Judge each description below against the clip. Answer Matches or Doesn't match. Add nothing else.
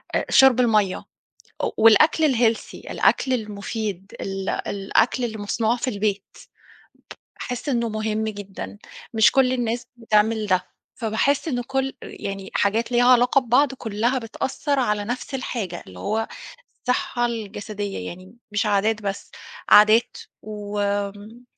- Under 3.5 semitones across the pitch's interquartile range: Matches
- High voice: Matches